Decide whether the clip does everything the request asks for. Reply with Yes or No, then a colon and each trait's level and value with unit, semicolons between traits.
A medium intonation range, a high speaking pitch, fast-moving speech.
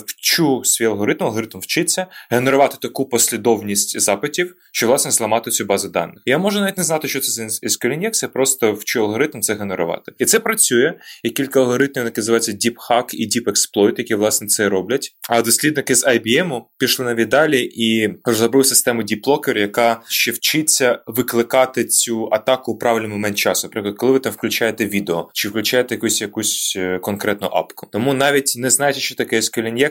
No: average, 3.5 semitones; low, 115 Hz; fast, 175 wpm